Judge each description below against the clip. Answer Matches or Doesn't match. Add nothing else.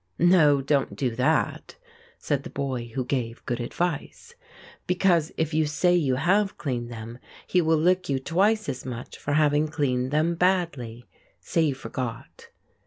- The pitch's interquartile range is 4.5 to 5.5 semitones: Matches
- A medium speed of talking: Matches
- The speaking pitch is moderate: Matches